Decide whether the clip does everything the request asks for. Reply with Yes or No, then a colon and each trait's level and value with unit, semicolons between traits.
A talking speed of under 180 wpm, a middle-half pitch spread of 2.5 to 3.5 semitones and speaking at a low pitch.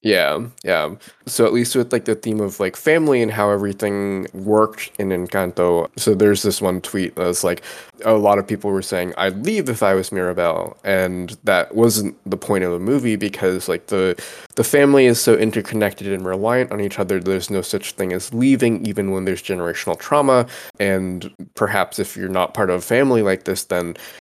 No: fast, 205 wpm; average, 3.0 semitones; low, 100 Hz